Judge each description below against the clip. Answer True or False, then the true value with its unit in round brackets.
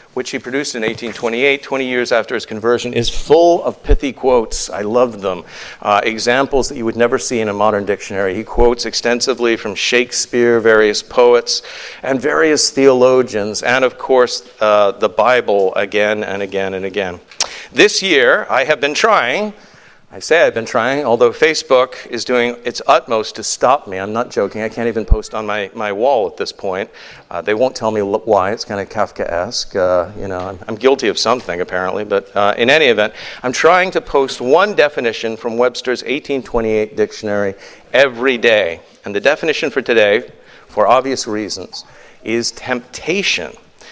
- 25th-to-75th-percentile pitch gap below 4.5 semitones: True (3.7 semitones)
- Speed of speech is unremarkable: True (180 wpm)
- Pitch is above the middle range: False (120 Hz)